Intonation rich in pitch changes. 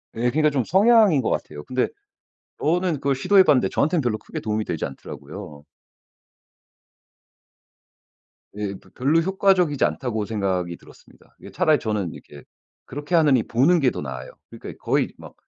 Yes: wide, 7.9 semitones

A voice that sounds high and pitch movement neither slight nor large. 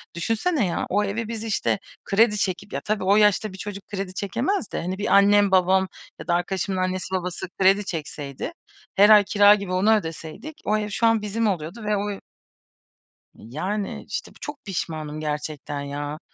Yes: high, 195 Hz; average, 3.0 semitones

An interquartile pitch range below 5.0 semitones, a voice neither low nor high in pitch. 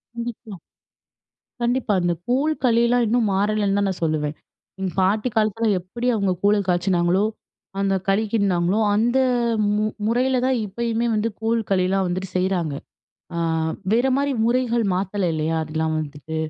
No: average, 4.4 semitones; high, 205 Hz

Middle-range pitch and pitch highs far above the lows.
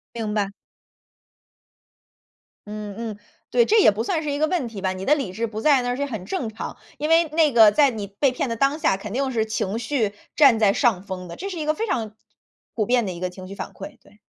No: high, 230 Hz; wide, 5.8 semitones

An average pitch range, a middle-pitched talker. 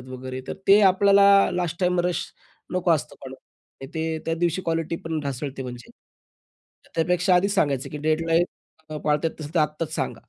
Yes: average, 3.1 semitones; medium, 165 Hz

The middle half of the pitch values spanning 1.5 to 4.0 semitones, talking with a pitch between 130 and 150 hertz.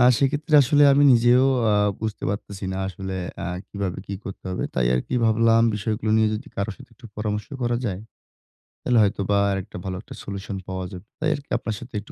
No: average, 3.5 semitones; low, 105 Hz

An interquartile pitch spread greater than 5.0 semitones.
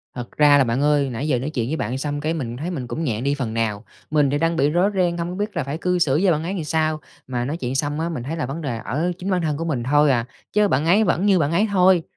No: average, 4.3 semitones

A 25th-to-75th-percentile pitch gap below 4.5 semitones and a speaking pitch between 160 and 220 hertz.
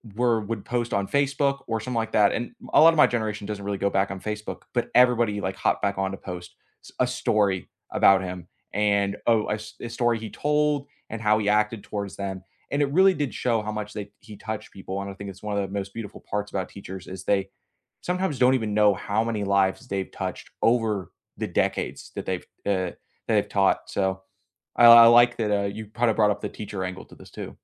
No: average, 3.1 semitones; low, 105 Hz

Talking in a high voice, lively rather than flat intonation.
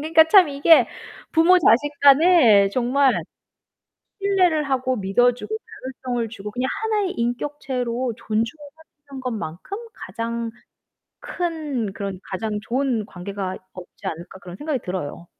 Yes: very high, 250 Hz; wide, 6.4 semitones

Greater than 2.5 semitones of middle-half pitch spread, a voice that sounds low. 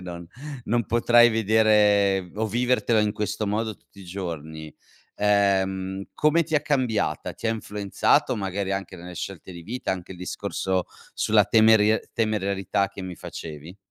Yes: average, 2.9 semitones; low, 100 Hz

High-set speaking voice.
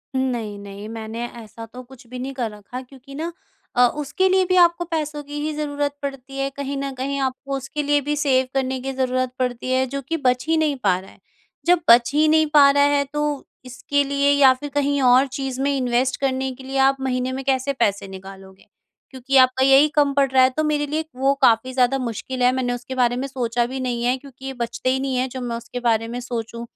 Yes: very high, 260 Hz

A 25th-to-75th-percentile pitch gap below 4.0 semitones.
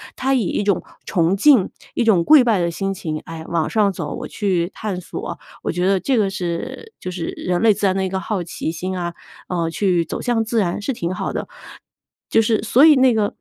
No: average, 4.3 semitones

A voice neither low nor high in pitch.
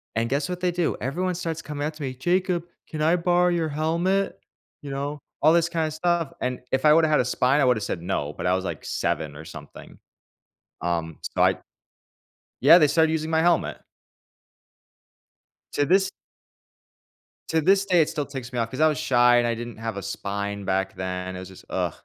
Yes: medium, 145 Hz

